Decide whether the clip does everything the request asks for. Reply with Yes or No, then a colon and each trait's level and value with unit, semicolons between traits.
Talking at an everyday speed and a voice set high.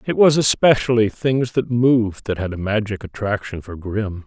No: average, 185 wpm; low, 115 Hz